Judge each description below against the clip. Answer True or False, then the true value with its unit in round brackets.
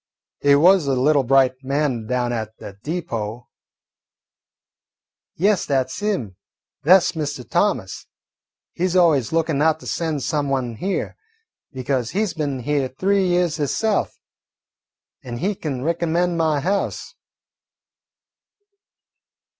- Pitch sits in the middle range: True (145 Hz)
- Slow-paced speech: True (130 wpm)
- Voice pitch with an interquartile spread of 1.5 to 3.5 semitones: False (5.1 semitones)